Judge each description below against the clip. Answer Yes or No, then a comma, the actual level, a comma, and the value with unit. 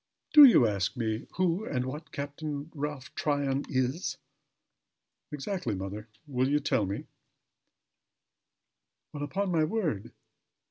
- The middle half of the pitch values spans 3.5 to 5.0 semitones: Yes, average, 4.1 semitones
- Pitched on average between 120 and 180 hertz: Yes, medium, 140 Hz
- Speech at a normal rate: No, slow, 120 wpm